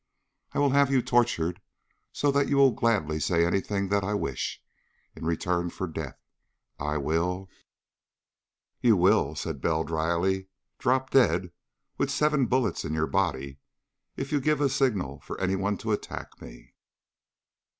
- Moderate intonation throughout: No, wide, 7.6 semitones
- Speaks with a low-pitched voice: Yes, very low, 95 Hz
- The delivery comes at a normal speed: Yes, average, 150 wpm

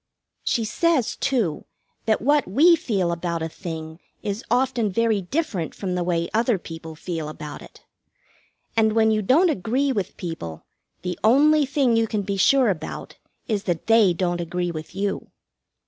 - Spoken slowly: No, average, 165 wpm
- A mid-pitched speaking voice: No, high, 205 Hz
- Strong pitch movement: Yes, wide, 5.9 semitones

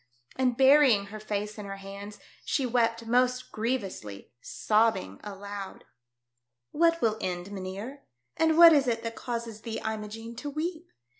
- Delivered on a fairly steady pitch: No, average, 4.1 semitones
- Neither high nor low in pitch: No, high, 225 Hz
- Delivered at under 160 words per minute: Yes, average, 150 wpm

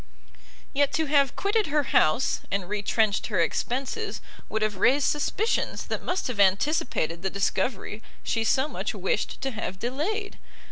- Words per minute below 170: Yes, average, 150 wpm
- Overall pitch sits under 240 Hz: No, very high, 250 Hz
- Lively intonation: Yes, wide, 6.8 semitones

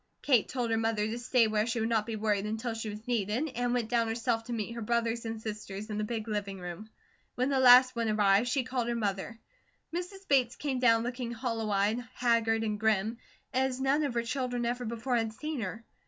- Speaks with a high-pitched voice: Yes, high, 230 Hz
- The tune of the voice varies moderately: No, narrow, 2.3 semitones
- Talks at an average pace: No, fast, 225 wpm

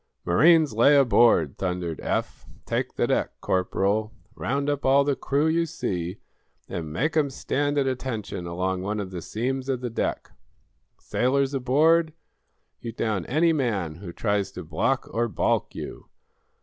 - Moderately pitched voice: No, low, 120 Hz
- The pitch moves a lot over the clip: Yes, wide, 6.8 semitones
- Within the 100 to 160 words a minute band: Yes, average, 155 wpm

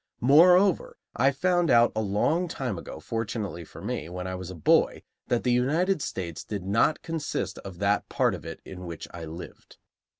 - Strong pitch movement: Yes, wide, 8.4 semitones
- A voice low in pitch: Yes, low, 110 Hz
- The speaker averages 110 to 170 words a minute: No, average, 190 wpm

